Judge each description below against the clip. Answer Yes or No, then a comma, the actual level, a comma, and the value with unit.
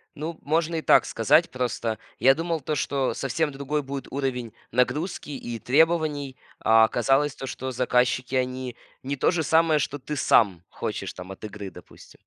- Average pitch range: Yes, average, 3.4 semitones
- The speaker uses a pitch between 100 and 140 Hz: Yes, low, 135 Hz